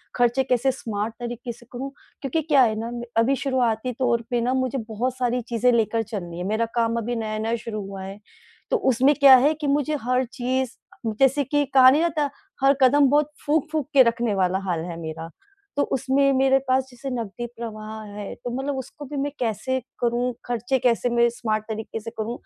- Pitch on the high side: Yes, high, 245 Hz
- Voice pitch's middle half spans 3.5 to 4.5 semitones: No, average, 3.0 semitones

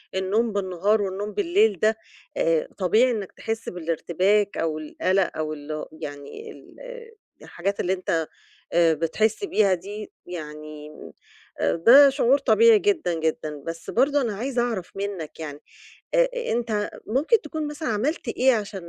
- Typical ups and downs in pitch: No, wide, 7.5 semitones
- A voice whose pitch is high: Yes, high, 205 Hz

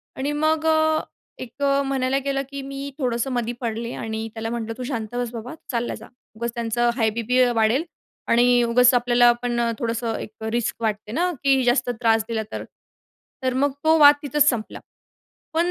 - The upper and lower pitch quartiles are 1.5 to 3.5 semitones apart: Yes, average, 3.0 semitones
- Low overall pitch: No, high, 245 Hz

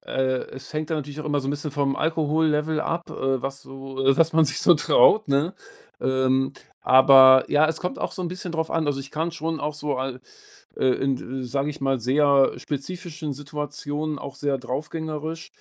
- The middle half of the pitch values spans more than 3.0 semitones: No, average, 2.7 semitones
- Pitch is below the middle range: No, medium, 145 Hz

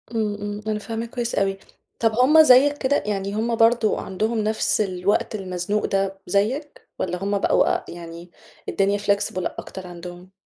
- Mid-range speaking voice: No, high, 205 Hz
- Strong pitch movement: No, average, 3.1 semitones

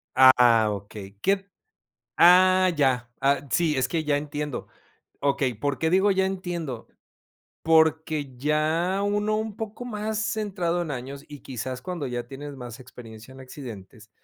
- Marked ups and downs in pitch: Yes, wide, 6.2 semitones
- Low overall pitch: No, medium, 145 Hz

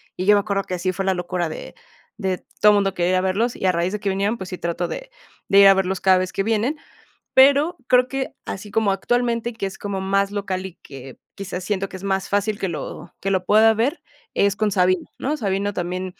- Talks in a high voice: Yes, high, 195 Hz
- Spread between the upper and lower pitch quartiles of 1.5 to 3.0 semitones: Yes, narrow, 2.4 semitones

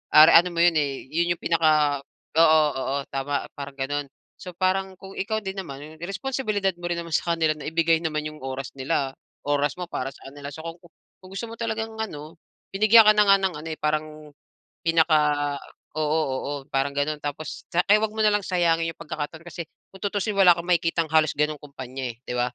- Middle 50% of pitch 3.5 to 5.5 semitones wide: Yes, average, 4.3 semitones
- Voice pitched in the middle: Yes, medium, 160 Hz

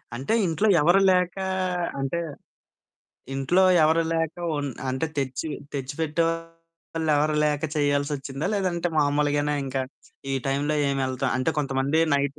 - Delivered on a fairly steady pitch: No, average, 3.1 semitones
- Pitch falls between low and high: Yes, medium, 150 Hz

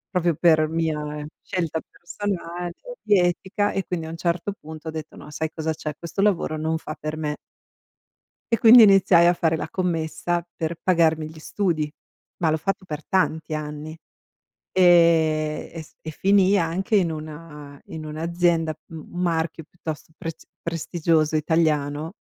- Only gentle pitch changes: Yes, narrow, 2.1 semitones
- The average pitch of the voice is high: No, medium, 165 Hz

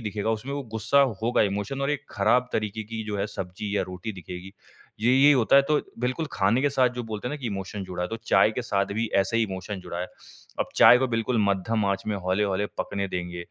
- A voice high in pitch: No, low, 105 Hz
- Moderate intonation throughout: Yes, average, 4.0 semitones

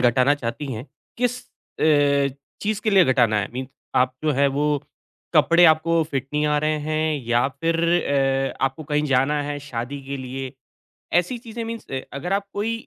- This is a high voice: No, medium, 145 Hz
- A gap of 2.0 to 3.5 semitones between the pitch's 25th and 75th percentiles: No, average, 3.9 semitones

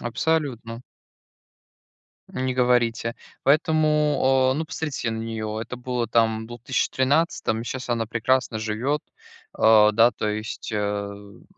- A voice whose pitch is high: No, low, 120 Hz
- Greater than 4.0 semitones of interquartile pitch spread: No, average, 2.9 semitones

